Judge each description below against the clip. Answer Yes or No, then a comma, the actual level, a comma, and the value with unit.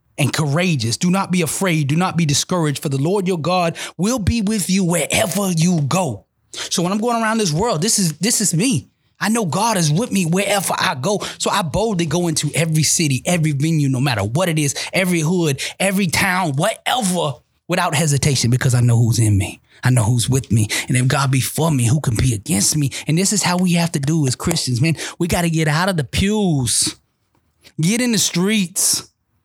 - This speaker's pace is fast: Yes, fast, 220 wpm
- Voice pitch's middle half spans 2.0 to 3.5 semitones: No, average, 4.8 semitones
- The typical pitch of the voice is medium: Yes, medium, 165 Hz